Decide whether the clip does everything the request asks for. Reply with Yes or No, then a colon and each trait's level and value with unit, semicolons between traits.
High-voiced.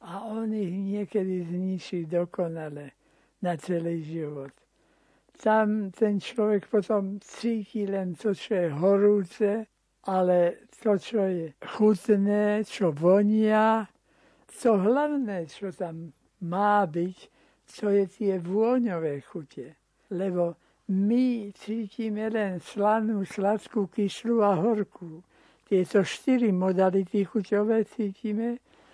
Yes: high, 200 Hz